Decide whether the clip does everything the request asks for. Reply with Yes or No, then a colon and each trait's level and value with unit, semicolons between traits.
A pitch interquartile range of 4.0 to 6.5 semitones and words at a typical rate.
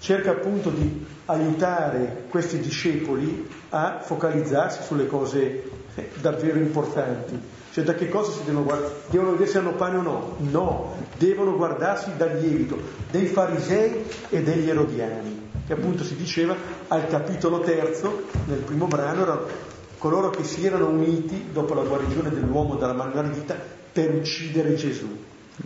No: average, 3.5 semitones; average, 145 wpm